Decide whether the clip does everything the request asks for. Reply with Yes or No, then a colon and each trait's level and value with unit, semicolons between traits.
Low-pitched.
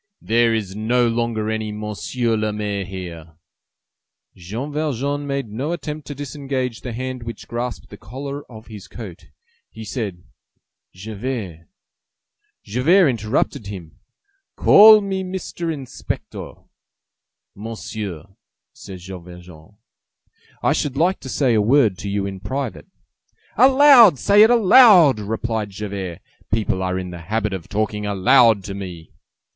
Yes: low, 110 Hz